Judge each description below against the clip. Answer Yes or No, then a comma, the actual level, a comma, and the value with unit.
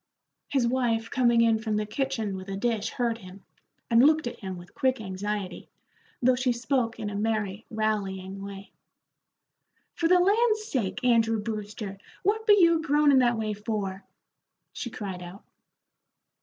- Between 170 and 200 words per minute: No, average, 155 wpm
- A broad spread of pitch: No, average, 4.2 semitones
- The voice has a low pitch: No, high, 225 Hz